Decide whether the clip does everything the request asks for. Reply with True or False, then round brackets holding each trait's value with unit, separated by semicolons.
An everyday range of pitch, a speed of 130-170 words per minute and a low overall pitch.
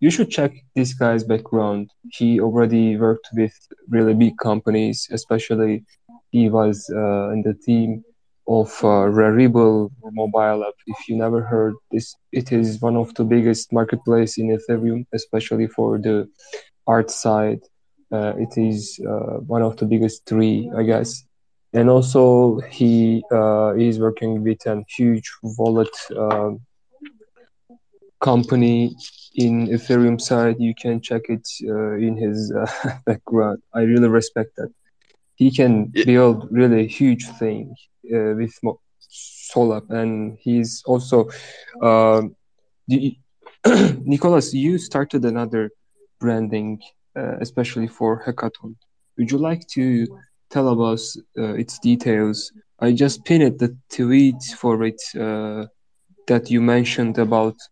False (1.6 semitones; 135 wpm; 115 Hz)